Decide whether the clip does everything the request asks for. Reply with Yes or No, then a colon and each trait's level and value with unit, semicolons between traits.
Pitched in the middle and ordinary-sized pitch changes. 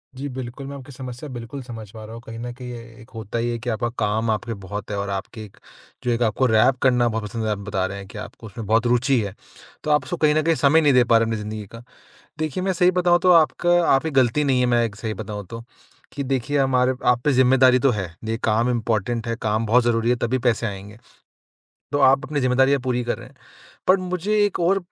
No: low, 120 Hz; average, 3.4 semitones